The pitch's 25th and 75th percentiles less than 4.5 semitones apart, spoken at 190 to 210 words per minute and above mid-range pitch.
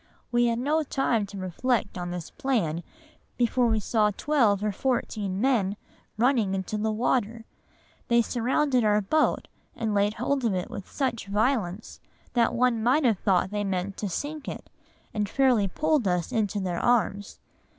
No: average, 4.0 semitones; average, 160 wpm; high, 220 Hz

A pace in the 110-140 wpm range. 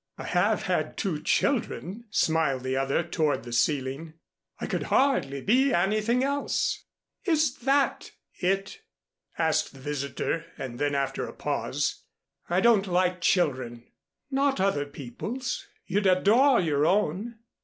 Yes: slow, 135 wpm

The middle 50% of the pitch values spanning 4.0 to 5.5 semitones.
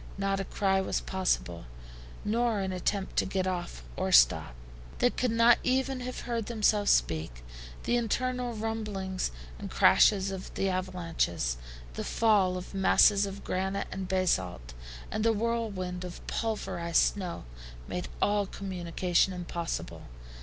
No: average, 3.4 semitones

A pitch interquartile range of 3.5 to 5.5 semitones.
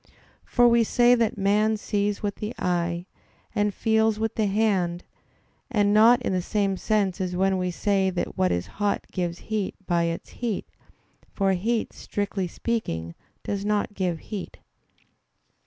No: average, 3.0 semitones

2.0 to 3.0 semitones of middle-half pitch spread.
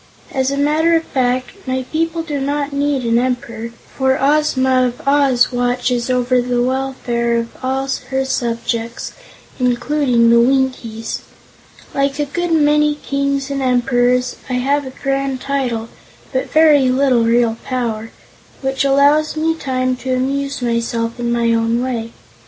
Yes: narrow, 2.5 semitones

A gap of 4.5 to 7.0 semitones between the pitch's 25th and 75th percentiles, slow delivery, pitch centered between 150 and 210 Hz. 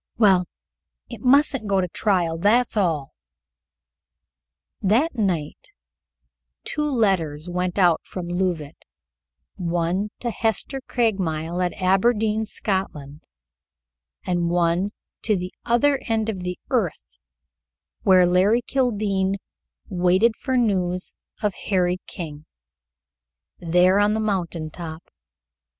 No: average, 3.8 semitones; slow, 110 wpm; high, 190 Hz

